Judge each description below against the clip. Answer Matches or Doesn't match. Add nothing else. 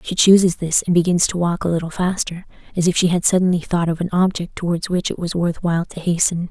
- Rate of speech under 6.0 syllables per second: Doesn't match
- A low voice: Doesn't match